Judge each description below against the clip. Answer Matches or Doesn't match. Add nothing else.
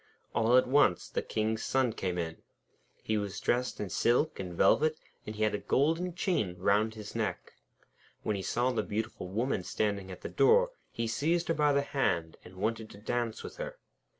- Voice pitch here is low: Matches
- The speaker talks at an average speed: Matches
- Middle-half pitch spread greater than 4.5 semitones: Matches